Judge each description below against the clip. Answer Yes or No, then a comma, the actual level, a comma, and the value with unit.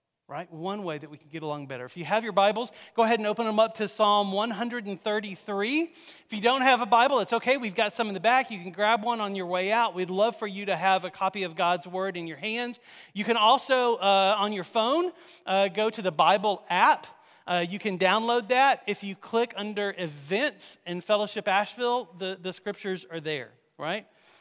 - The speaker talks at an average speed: No, fast, 225 wpm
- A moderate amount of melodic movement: Yes, average, 3.8 semitones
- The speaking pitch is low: No, high, 205 Hz